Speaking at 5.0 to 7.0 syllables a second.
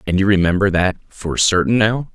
Yes: 5.2 syllables/s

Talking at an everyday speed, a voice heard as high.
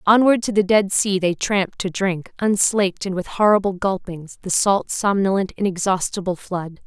Yes: average, 165 wpm; high, 195 Hz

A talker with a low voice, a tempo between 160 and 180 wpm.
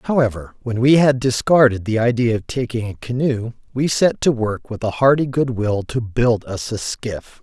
No: low, 120 Hz; average, 200 wpm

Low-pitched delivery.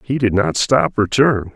Yes: low, 110 Hz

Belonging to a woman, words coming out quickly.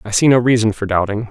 No: male; fast, 275 wpm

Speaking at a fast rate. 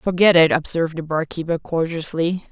No: average, 145 wpm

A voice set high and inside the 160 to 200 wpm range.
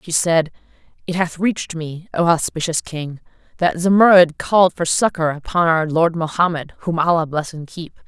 No: medium, 165 Hz; average, 170 wpm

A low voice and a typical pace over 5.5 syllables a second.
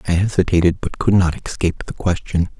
Yes: very low, 90 Hz; 6.2 syllables/s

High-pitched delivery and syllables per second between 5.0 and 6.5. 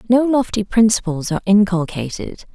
Yes: high, 205 Hz; 5.3 syllables/s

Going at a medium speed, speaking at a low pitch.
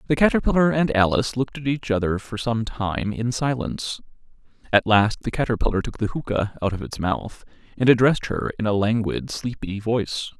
Yes: average, 185 wpm; low, 115 Hz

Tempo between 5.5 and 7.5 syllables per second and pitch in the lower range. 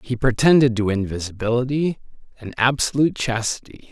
Yes: 5.6 syllables/s; low, 120 Hz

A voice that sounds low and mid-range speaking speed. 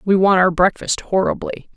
No: medium, 185 Hz; average, 170 wpm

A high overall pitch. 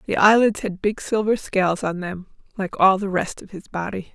Yes: high, 195 Hz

